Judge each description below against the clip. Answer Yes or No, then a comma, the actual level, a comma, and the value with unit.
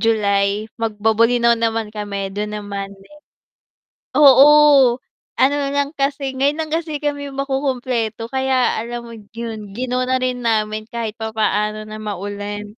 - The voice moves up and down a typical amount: Yes, average, 4.0 semitones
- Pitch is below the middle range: No, high, 230 Hz